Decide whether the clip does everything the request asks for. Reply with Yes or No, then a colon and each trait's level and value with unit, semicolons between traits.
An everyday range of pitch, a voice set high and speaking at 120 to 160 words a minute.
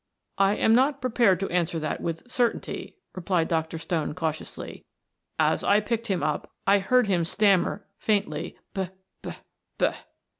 Yes: average, 4.5 semitones; high, 195 Hz; average, 150 wpm